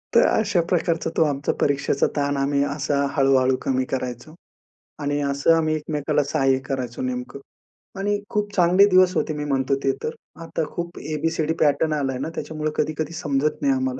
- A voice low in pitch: No, medium, 145 Hz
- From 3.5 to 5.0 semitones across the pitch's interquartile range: No, average, 3.0 semitones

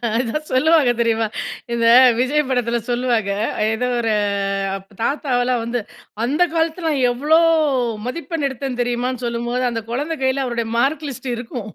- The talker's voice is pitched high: Yes, very high, 250 Hz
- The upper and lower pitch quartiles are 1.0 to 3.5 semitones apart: Yes, average, 3.0 semitones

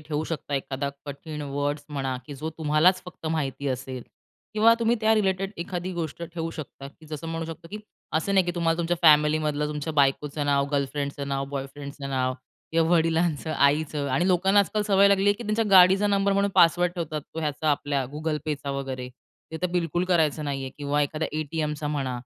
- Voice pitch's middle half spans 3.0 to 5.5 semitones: Yes, average, 3.7 semitones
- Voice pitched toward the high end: No, medium, 155 Hz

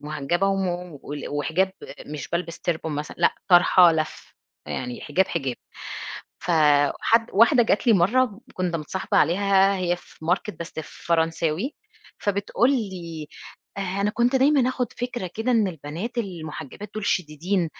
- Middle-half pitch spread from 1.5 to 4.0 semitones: No, average, 4.6 semitones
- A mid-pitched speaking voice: Yes, medium, 180 Hz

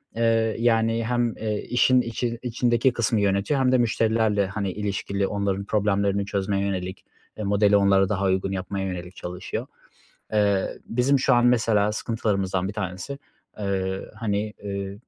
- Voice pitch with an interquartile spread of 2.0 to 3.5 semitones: Yes, average, 2.7 semitones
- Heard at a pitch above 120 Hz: No, low, 105 Hz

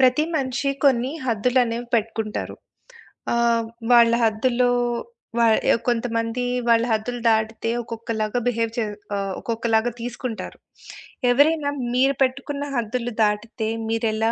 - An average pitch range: No, narrow, 2.0 semitones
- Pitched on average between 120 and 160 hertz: No, high, 230 Hz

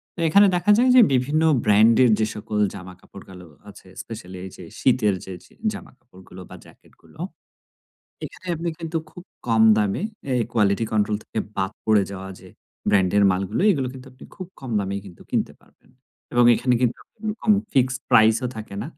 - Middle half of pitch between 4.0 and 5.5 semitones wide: Yes, average, 4.7 semitones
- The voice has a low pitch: Yes, low, 110 Hz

